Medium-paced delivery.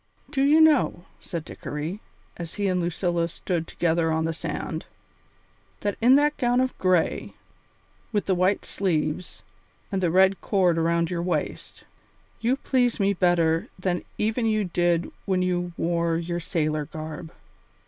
Yes: average, 150 wpm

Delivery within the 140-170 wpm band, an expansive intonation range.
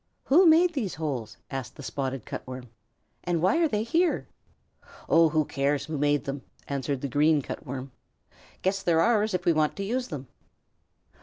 No: average, 180 wpm; wide, 7.1 semitones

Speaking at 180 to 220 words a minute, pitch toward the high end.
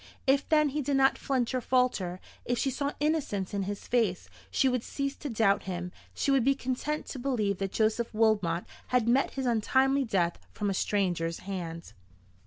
Yes: average, 190 wpm; high, 235 Hz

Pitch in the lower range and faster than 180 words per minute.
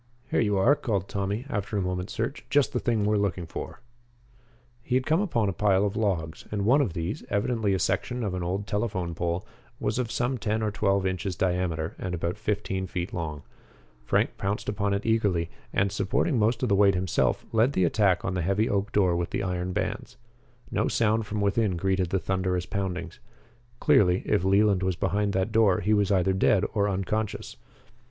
Yes: low, 100 Hz; average, 200 wpm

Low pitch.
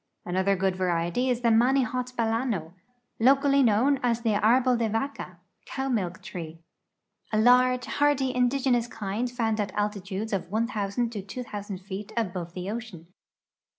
No: high, 225 Hz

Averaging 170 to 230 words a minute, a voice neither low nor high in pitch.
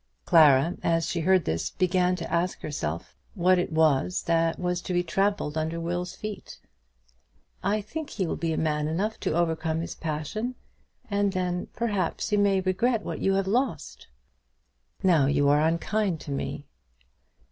No: average, 160 wpm; medium, 175 Hz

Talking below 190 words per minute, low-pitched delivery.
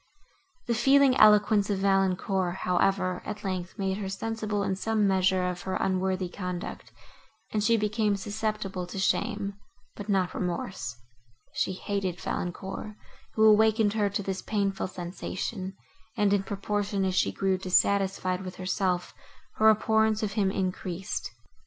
No: average, 140 wpm; high, 195 Hz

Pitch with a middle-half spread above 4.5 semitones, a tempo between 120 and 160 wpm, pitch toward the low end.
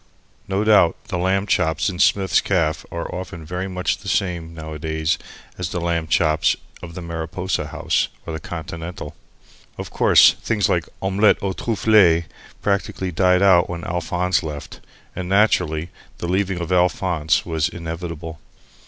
No: narrow, 2.6 semitones; average, 150 wpm; very low, 90 Hz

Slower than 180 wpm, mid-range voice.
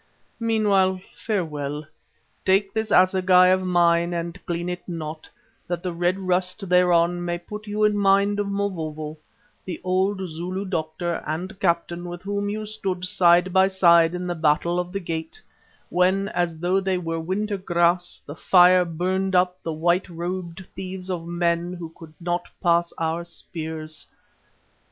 Yes: average, 155 wpm; medium, 180 Hz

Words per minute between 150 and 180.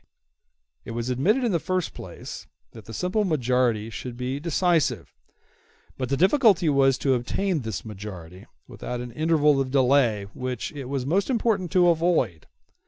Yes: average, 160 wpm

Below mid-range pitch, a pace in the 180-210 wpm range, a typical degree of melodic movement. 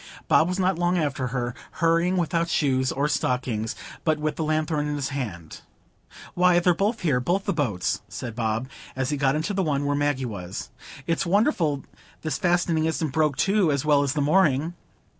No: medium, 150 Hz; average, 185 wpm; average, 4.6 semitones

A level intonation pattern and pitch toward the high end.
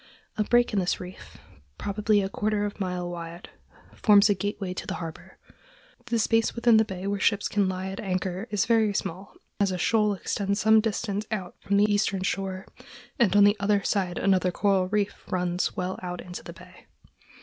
Yes: narrow, 2.3 semitones; high, 200 Hz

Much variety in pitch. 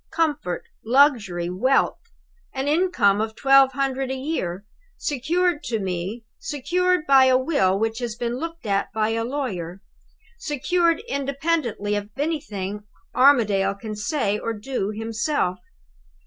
Yes: wide, 5.9 semitones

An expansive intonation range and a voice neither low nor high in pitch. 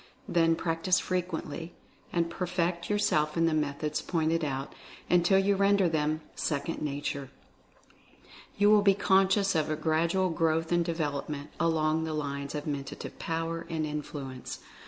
No: average, 2.7 semitones; medium, 165 Hz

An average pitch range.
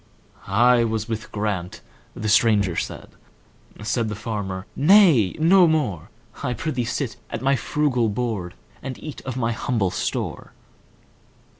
Yes: average, 4.1 semitones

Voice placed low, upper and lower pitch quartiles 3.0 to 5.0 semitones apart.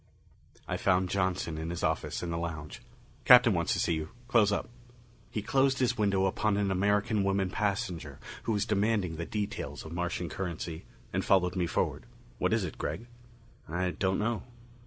Yes: very low, 95 Hz; average, 3.6 semitones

